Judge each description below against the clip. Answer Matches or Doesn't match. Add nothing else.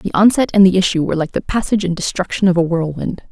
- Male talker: Doesn't match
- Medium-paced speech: Doesn't match